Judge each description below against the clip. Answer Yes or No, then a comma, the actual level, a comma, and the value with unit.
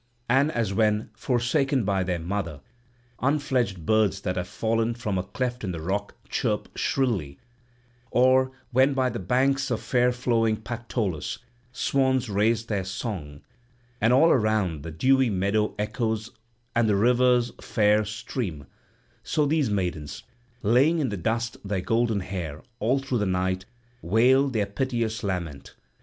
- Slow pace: No, average, 145 wpm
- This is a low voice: Yes, low, 110 Hz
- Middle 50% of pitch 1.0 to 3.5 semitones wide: No, average, 4.6 semitones